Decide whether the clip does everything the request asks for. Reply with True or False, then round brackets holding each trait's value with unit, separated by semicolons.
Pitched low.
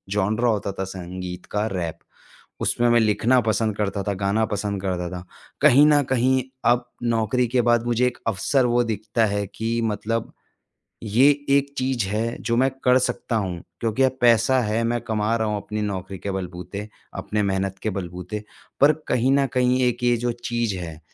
True (110 Hz)